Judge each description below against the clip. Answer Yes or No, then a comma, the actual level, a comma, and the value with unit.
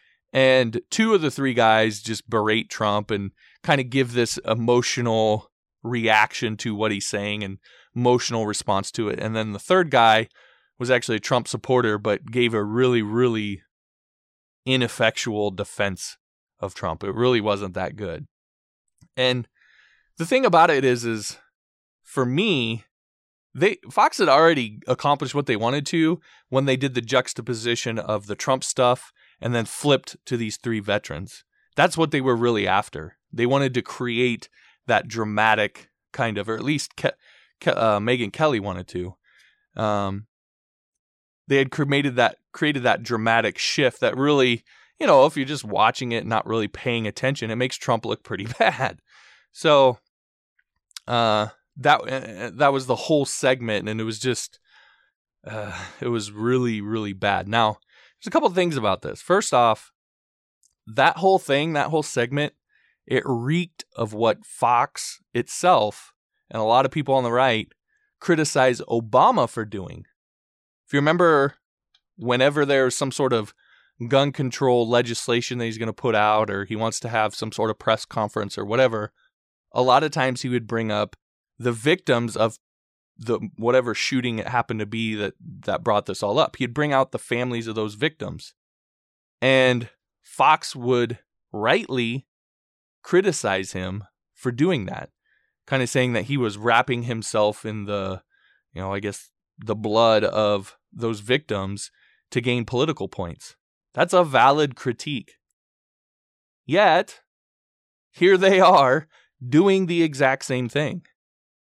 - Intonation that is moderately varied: Yes, average, 4.0 semitones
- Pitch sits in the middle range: No, low, 120 Hz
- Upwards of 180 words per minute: No, average, 160 wpm